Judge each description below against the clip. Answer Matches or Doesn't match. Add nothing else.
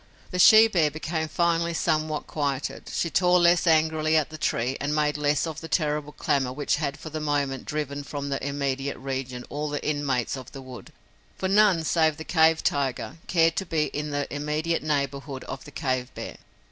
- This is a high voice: Doesn't match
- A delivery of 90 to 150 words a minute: Doesn't match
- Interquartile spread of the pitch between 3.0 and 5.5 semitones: Doesn't match